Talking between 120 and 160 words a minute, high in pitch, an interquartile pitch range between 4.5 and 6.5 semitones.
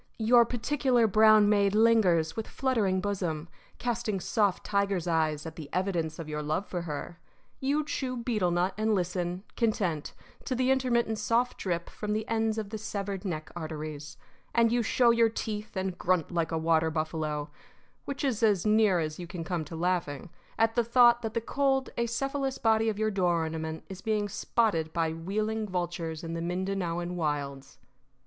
No: average, 175 wpm; high, 195 Hz; average, 5.2 semitones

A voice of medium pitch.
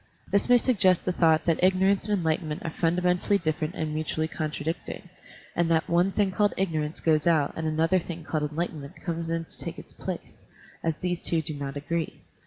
Yes: medium, 165 Hz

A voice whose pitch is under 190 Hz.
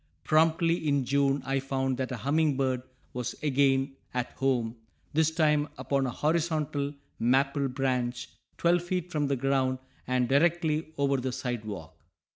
Yes: low, 135 Hz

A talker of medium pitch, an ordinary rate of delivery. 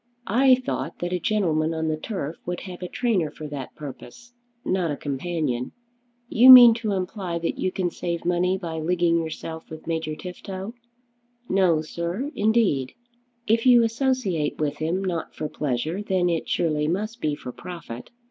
Yes: medium, 175 Hz; average, 165 wpm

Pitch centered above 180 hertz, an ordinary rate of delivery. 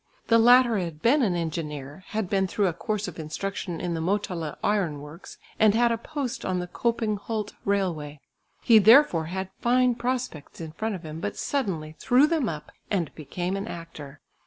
Yes: high, 190 Hz; average, 185 wpm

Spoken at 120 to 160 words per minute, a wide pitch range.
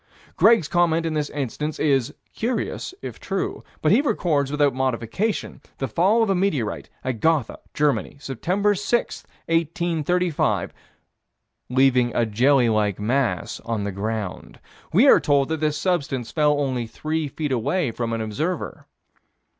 Yes: average, 145 wpm; wide, 5.7 semitones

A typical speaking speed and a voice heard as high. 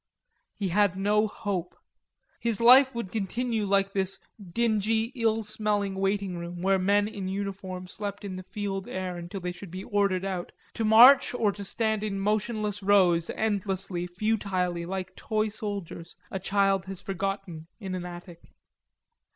Yes: average, 155 wpm; high, 195 Hz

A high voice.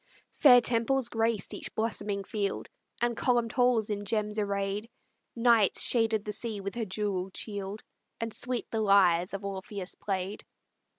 Yes: high, 210 Hz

